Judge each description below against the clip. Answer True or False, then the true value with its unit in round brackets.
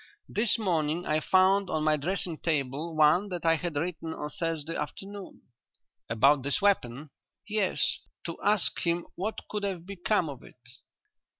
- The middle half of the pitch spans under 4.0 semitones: False (4.3 semitones)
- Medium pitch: True (170 Hz)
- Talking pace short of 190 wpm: True (155 wpm)